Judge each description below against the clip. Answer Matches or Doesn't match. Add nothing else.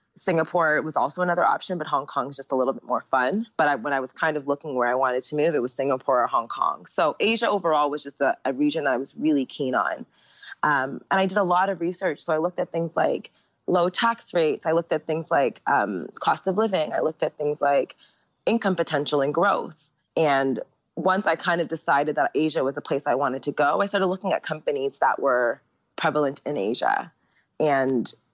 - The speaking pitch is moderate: Matches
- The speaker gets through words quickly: Matches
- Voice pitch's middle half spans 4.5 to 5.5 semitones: Matches